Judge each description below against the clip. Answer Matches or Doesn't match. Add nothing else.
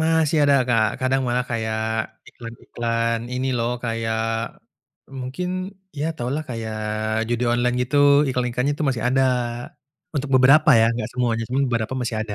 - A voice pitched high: Doesn't match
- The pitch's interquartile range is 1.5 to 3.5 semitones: Matches